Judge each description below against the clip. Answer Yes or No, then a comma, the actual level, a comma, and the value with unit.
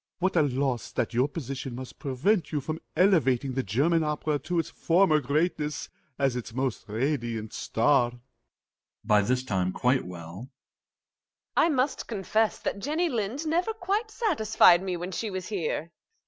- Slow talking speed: No, average, 160 wpm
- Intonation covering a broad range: Yes, wide, 7.6 semitones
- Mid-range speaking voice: Yes, medium, 150 Hz